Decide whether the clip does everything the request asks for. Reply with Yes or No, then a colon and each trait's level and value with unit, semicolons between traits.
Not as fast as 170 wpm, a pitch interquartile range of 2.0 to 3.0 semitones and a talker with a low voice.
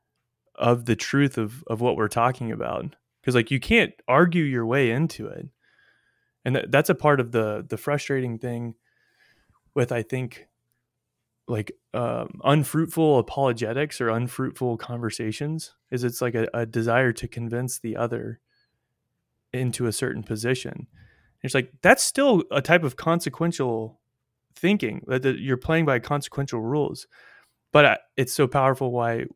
No: average, 155 wpm; average, 3.7 semitones; low, 130 Hz